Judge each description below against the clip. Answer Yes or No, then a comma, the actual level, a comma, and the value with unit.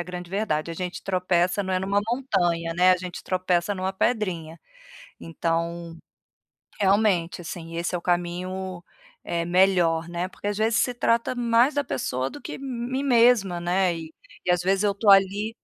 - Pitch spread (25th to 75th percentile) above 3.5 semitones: No, average, 3.0 semitones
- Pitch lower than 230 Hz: Yes, medium, 185 Hz